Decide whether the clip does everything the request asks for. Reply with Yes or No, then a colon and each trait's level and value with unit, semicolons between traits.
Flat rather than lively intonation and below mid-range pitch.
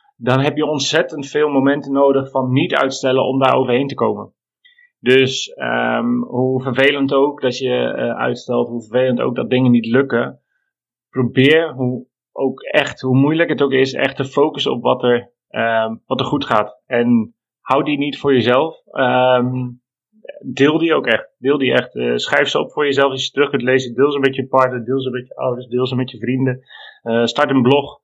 Yes: narrow, 2.0 semitones; low, 130 Hz